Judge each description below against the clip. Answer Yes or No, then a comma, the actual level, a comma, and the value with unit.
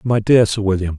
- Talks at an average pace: No, fast, 245 wpm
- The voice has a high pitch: No, low, 105 Hz